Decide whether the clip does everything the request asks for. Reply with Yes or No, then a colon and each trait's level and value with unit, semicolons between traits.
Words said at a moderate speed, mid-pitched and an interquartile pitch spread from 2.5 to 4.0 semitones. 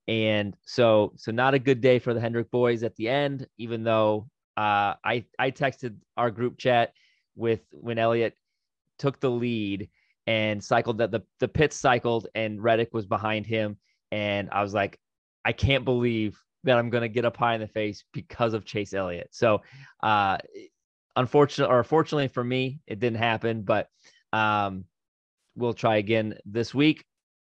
No: average, 170 wpm; low, 115 Hz; average, 2.8 semitones